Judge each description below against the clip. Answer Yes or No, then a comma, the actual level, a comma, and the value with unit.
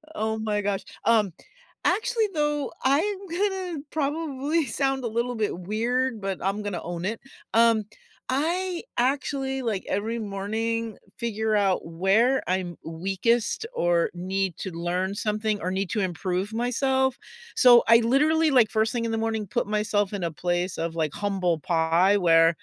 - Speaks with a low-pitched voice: No, high, 220 Hz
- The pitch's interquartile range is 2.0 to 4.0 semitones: No, wide, 5.6 semitones